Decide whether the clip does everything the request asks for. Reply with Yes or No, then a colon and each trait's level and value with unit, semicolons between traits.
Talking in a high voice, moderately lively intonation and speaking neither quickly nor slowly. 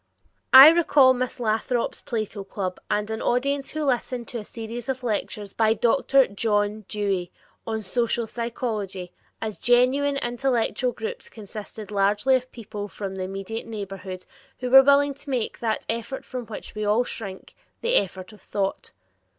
Yes: high, 225 Hz; average, 3.7 semitones; average, 160 wpm